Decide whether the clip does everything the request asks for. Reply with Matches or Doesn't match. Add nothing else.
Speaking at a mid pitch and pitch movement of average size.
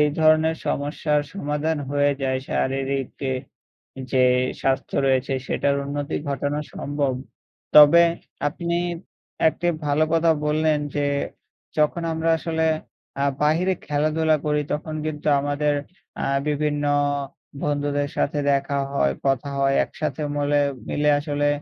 Doesn't match